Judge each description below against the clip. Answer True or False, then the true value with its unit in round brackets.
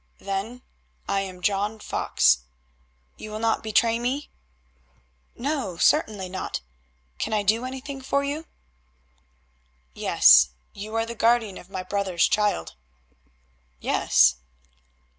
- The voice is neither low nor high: False (215 Hz)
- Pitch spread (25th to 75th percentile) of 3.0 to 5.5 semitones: True (4.1 semitones)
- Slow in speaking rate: True (115 wpm)